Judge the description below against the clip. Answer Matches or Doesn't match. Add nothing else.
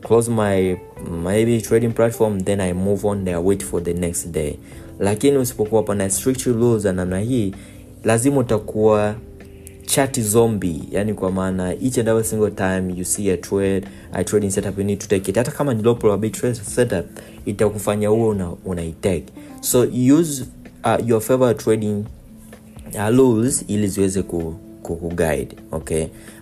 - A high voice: Doesn't match